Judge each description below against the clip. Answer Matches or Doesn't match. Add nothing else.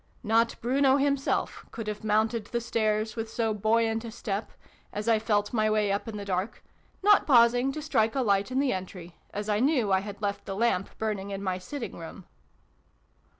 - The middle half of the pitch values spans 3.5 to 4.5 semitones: Doesn't match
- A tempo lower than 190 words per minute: Doesn't match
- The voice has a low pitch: Doesn't match